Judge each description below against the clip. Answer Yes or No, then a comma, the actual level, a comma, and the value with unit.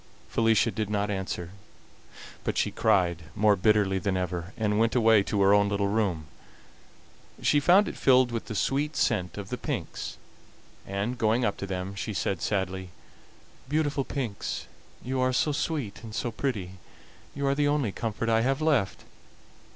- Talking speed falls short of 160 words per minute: No, average, 165 wpm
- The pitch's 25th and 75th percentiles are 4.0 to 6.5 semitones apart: Yes, average, 4.8 semitones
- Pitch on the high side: No, low, 110 Hz